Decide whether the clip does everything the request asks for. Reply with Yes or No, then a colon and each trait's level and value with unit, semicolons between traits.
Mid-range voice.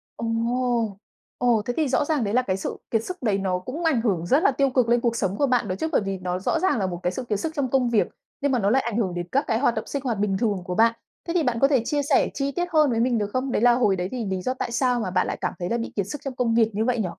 No: high, 235 Hz